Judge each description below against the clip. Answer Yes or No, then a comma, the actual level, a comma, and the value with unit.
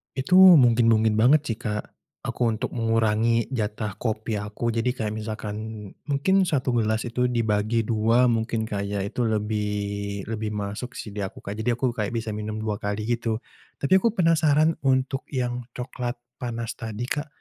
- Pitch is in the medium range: No, low, 115 Hz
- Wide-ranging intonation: No, narrow, 2.6 semitones